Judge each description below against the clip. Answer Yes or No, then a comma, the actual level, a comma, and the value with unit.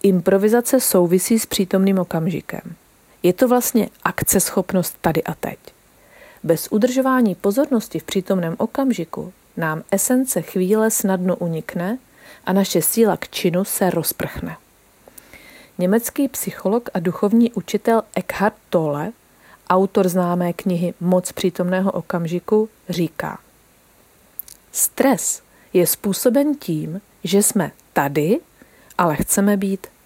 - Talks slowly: Yes, slow, 110 wpm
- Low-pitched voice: No, high, 195 Hz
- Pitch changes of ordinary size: Yes, average, 3.7 semitones